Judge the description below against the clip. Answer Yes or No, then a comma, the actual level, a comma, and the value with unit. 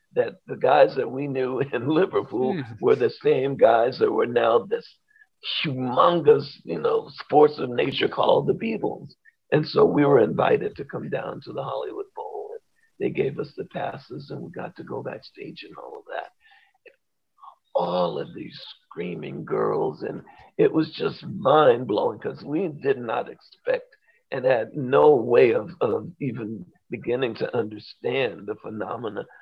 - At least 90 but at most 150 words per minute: No, average, 165 wpm